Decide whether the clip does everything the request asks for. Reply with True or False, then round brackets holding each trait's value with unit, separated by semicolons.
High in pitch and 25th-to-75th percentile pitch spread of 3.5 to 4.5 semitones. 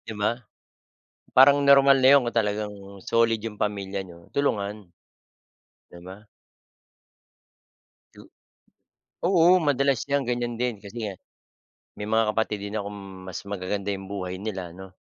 False (105 Hz; 3.8 semitones)